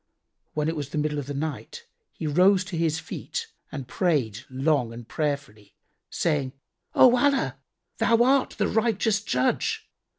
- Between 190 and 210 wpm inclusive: No, average, 155 wpm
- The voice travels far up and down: Yes, wide, 6.8 semitones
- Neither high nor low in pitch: Yes, medium, 155 Hz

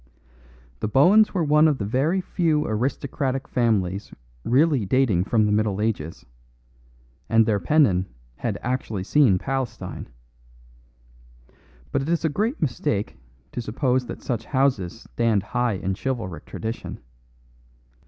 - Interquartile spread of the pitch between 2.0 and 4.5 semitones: No, average, 5.2 semitones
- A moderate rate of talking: No, slow, 130 wpm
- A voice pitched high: No, low, 120 Hz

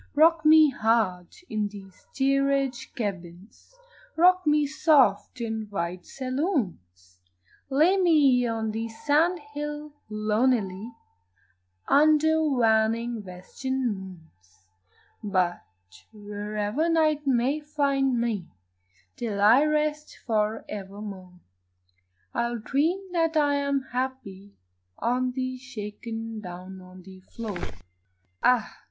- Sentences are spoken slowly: Yes, slow, 100 wpm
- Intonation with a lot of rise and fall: Yes, wide, 6.1 semitones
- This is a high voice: Yes, high, 240 Hz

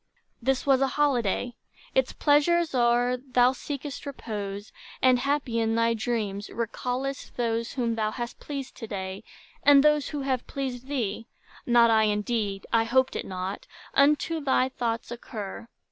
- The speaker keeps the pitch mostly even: No, average, 3.3 semitones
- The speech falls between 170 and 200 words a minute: No, average, 145 wpm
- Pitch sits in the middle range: No, high, 245 Hz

